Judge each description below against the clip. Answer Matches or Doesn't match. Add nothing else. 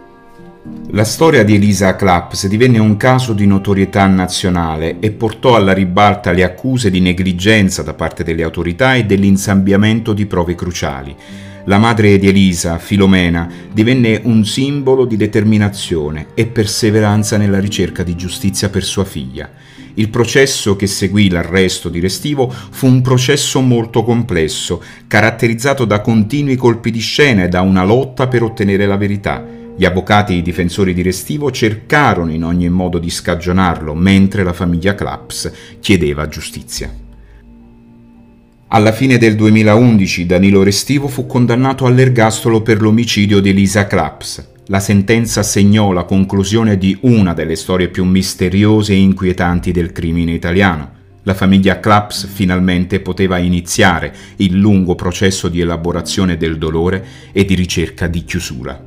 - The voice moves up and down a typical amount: Matches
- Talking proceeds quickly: Doesn't match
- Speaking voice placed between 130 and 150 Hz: Doesn't match